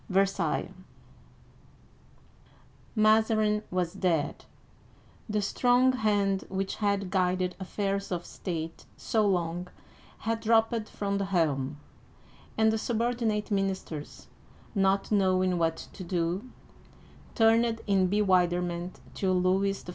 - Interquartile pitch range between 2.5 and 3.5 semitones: Yes, average, 2.9 semitones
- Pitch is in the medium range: No, high, 195 Hz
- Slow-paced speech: Yes, slow, 105 wpm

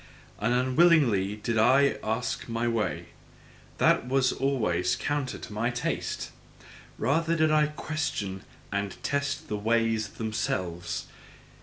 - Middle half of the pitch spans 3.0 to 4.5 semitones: No, average, 5.0 semitones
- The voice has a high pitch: No, low, 115 Hz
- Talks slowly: Yes, slow, 125 wpm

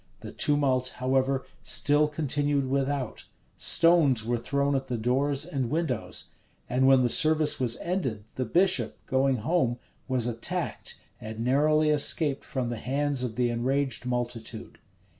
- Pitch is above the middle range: No, low, 135 Hz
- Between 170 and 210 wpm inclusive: No, average, 140 wpm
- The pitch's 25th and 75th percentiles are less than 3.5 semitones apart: Yes, average, 2.9 semitones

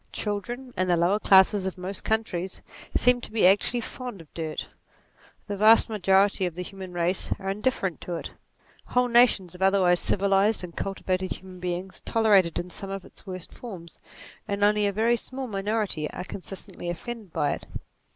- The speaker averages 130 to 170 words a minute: No, average, 180 wpm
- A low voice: No, high, 195 Hz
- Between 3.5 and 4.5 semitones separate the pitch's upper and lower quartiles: No, average, 2.9 semitones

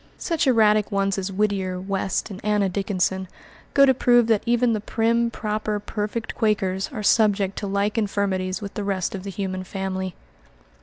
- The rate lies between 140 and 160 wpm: No, average, 170 wpm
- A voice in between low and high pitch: No, high, 200 Hz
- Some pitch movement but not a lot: No, narrow, 2.3 semitones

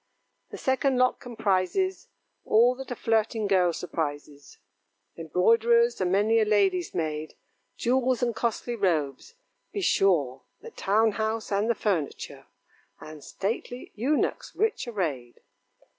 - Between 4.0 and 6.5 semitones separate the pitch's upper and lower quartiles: Yes, average, 5.3 semitones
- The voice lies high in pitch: Yes, high, 215 Hz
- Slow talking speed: Yes, slow, 125 wpm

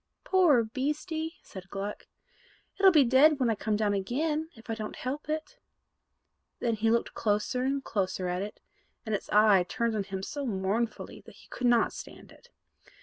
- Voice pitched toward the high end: Yes, high, 230 Hz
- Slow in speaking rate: No, average, 180 wpm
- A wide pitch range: Yes, wide, 5.8 semitones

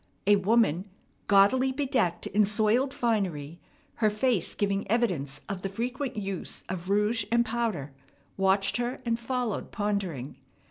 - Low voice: No, high, 210 Hz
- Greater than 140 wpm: No, slow, 135 wpm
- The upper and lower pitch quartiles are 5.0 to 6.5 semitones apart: No, average, 3.7 semitones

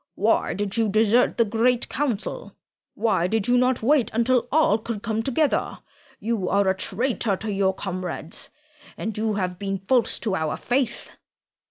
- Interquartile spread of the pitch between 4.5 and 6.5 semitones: No, average, 3.6 semitones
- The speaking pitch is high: Yes, high, 220 Hz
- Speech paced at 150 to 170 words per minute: Yes, average, 165 wpm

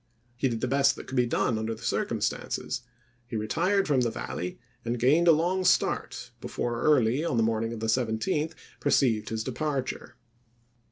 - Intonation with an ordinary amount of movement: Yes, average, 4.7 semitones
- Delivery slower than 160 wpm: No, average, 180 wpm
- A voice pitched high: No, low, 125 Hz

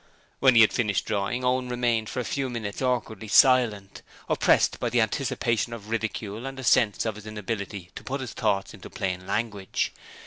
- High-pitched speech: No, low, 115 Hz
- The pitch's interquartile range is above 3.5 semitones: No, average, 3.2 semitones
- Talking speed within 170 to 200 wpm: Yes, average, 185 wpm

